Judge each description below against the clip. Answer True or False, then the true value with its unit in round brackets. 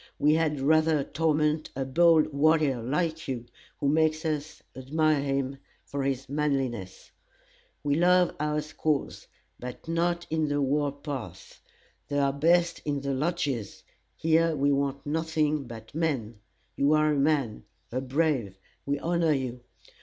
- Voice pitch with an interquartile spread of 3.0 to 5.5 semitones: False (2.6 semitones)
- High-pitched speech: False (145 Hz)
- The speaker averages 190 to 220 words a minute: False (145 wpm)